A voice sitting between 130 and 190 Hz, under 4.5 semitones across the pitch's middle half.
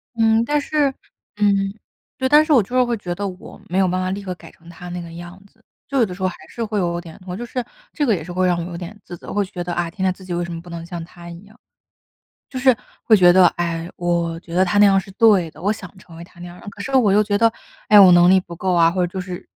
Yes: medium, 185 Hz; average, 3.2 semitones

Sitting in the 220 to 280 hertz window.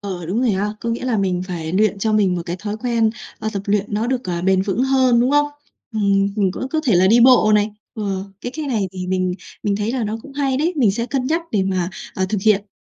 No: high, 210 Hz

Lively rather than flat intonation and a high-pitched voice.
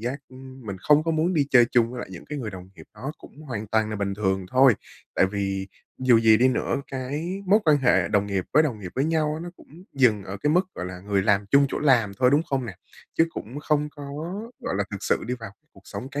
No: wide, 6.3 semitones; low, 125 Hz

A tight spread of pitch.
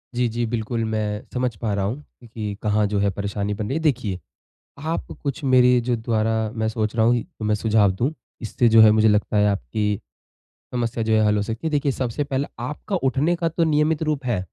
No: average, 3.6 semitones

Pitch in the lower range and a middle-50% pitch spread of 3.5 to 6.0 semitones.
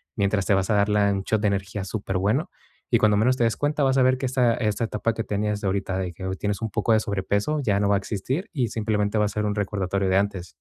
No: low, 105 Hz; narrow, 2.4 semitones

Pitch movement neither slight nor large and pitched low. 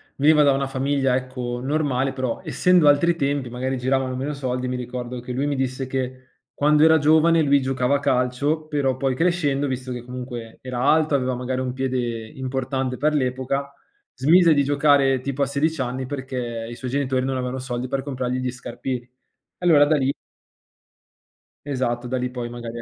No: narrow, 2.1 semitones; low, 130 Hz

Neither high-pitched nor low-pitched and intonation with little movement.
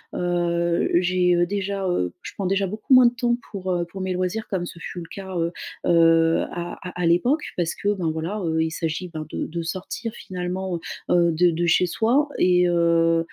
Yes: medium, 180 Hz; narrow, 2.2 semitones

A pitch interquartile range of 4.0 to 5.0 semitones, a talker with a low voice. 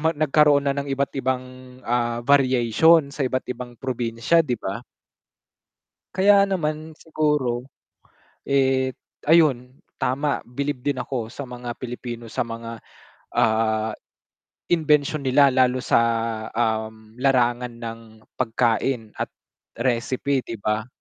No: average, 3.2 semitones; low, 130 Hz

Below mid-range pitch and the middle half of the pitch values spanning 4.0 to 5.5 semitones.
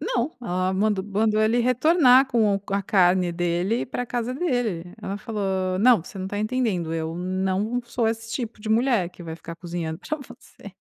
No: high, 210 Hz; average, 4.5 semitones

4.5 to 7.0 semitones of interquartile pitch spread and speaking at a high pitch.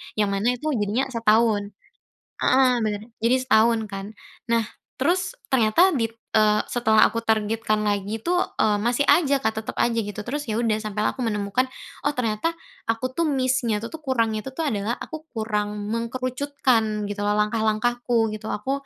No: average, 3.2 semitones; high, 225 Hz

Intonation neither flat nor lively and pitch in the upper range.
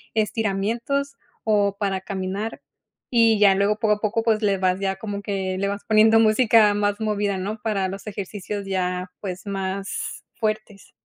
No: narrow, 1.9 semitones; high, 205 Hz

